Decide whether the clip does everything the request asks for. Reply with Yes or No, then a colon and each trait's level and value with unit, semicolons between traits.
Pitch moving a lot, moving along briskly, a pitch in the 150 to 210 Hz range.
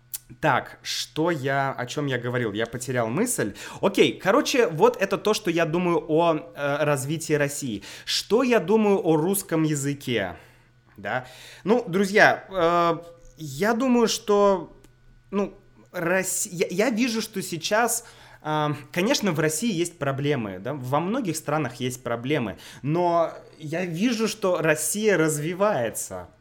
No: wide, 6.3 semitones; average, 135 wpm; medium, 160 Hz